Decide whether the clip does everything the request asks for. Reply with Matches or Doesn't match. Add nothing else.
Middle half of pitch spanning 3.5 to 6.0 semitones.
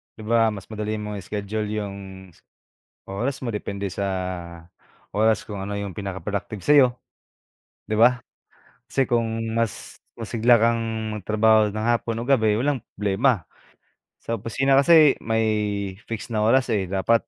Doesn't match